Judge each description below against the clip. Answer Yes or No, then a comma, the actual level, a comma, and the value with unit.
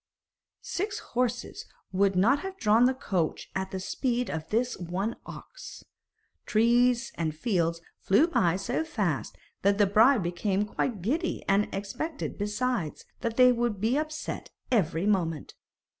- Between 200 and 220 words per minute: No, average, 145 wpm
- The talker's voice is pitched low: No, high, 215 Hz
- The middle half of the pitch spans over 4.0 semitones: Yes, average, 4.9 semitones